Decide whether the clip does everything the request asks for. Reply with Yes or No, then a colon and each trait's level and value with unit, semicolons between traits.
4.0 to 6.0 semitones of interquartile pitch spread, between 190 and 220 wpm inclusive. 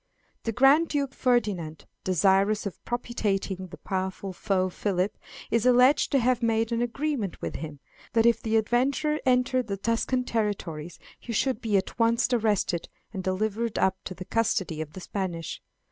No: average, 4.3 semitones; average, 160 wpm